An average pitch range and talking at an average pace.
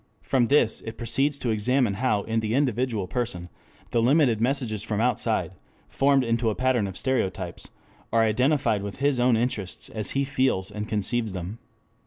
Yes: average, 3.7 semitones; average, 170 wpm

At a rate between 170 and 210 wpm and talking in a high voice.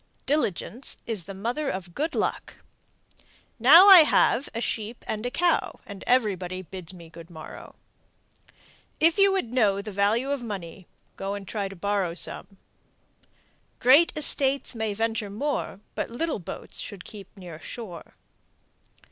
No: average, 145 wpm; high, 215 Hz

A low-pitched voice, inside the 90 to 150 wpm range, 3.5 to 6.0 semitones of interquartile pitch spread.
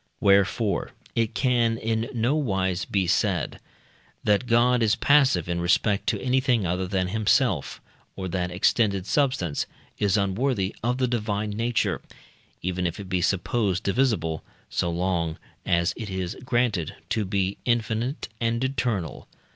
Yes: low, 105 Hz; average, 140 wpm; average, 4.3 semitones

